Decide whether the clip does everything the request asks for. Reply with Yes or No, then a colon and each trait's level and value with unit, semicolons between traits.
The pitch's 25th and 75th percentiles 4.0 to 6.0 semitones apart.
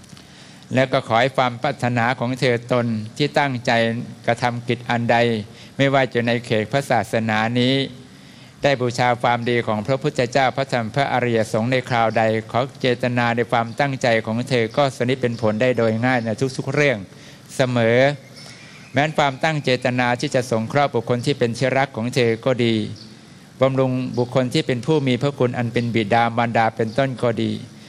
No: narrow, 2.5 semitones